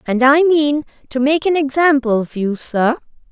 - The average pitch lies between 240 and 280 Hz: Yes, very high, 270 Hz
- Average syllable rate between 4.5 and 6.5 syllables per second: Yes, 4.6 syllables/s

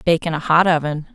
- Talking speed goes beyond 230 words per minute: Yes, fast, 260 wpm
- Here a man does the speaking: No, female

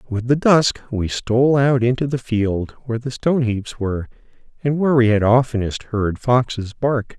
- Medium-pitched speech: No, low, 120 Hz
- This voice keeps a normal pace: Yes, average, 185 wpm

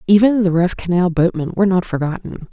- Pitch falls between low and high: Yes, medium, 180 Hz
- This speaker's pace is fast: No, average, 190 wpm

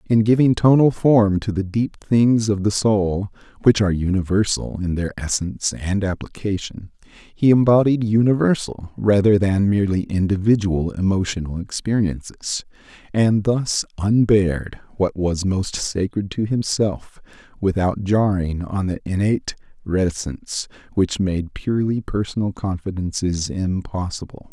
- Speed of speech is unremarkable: No, slow, 120 wpm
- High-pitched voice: No, low, 100 Hz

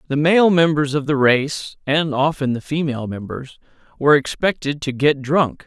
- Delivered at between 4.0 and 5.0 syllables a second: Yes, 4.8 syllables/s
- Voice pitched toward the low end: No, medium, 145 Hz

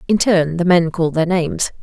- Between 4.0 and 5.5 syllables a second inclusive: No, 5.7 syllables/s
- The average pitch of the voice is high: No, medium, 175 Hz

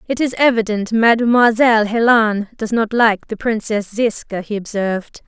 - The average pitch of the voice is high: Yes, high, 220 Hz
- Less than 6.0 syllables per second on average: Yes, 4.8 syllables/s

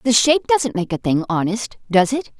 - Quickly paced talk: Yes, fast, 225 wpm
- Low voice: No, high, 225 Hz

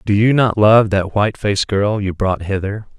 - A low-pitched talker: Yes, low, 105 Hz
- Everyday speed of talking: No, fast, 220 wpm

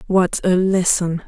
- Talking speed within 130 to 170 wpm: Yes, average, 140 wpm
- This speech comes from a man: No, female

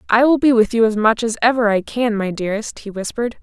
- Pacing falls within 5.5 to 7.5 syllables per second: Yes, 6.3 syllables/s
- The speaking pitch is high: Yes, high, 225 Hz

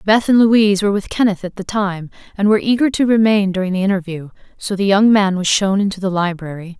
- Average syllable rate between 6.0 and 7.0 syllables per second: Yes, 6.2 syllables/s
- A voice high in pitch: Yes, high, 200 Hz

